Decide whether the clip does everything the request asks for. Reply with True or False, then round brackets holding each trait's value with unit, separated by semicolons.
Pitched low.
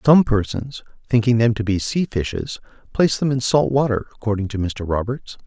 True (120 Hz)